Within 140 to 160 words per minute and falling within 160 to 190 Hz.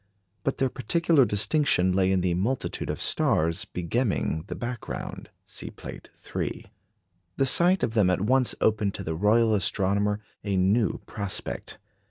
No: average, 150 wpm; low, 105 Hz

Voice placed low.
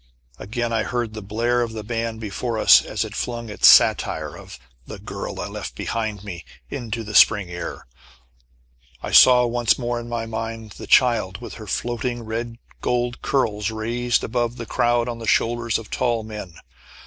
Yes: low, 115 Hz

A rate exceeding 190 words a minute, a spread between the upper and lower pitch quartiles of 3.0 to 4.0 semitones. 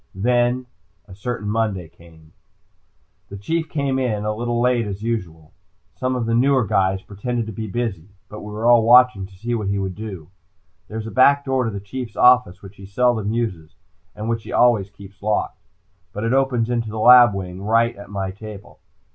Yes: average, 200 wpm; average, 3.6 semitones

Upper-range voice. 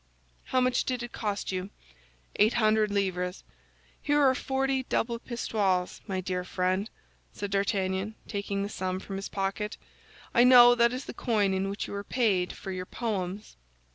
Yes: high, 205 Hz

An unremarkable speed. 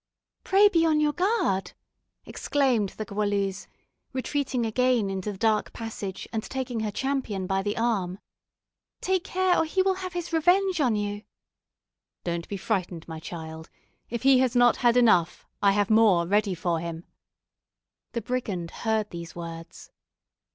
Yes: average, 155 wpm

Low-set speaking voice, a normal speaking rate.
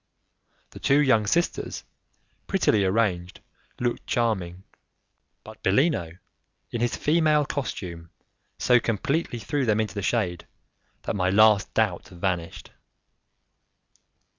No: low, 110 Hz; slow, 110 wpm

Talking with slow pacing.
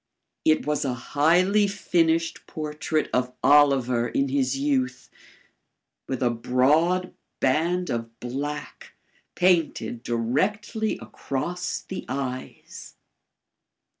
Yes: slow, 95 wpm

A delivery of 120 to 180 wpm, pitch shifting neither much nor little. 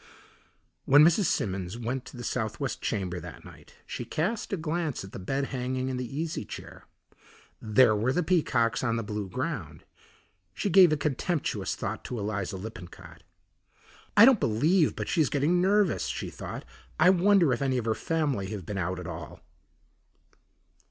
No: average, 170 wpm; wide, 7.5 semitones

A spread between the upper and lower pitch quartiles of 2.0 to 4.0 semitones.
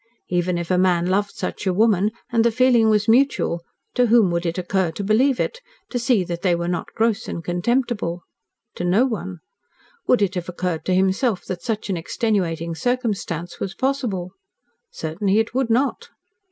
No: average, 4.7 semitones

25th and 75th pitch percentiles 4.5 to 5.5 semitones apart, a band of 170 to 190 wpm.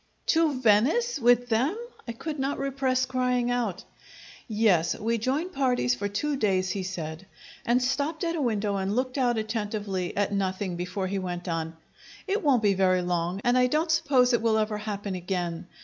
Yes: average, 5.2 semitones; average, 180 wpm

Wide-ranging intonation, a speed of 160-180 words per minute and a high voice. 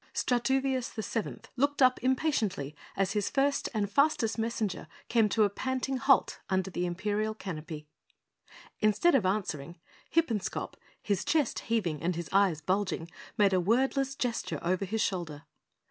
No: wide, 5.7 semitones; average, 145 wpm; high, 215 Hz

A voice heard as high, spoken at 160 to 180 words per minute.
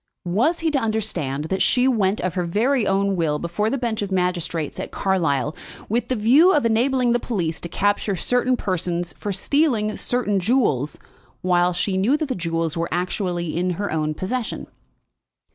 Yes: high, 195 Hz; average, 175 wpm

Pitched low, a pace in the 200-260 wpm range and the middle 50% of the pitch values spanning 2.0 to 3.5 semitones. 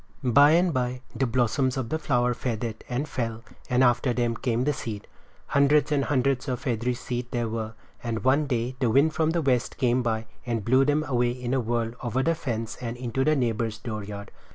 Yes: low, 125 Hz; fast, 205 wpm; narrow, 2.6 semitones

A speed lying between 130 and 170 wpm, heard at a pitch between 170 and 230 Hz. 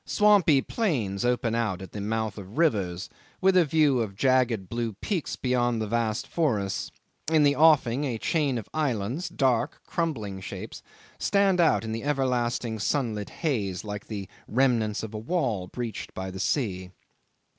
No: average, 160 wpm; low, 120 Hz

